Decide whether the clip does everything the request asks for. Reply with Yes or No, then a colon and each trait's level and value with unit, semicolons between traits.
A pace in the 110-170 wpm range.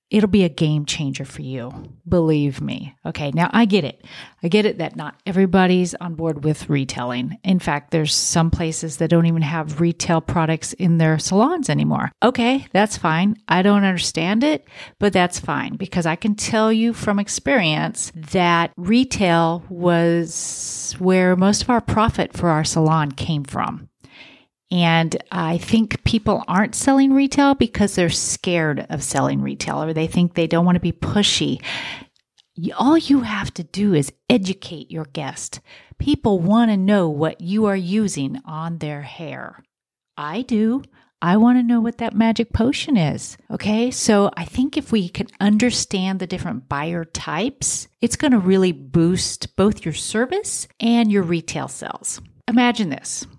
Yes: average, 165 wpm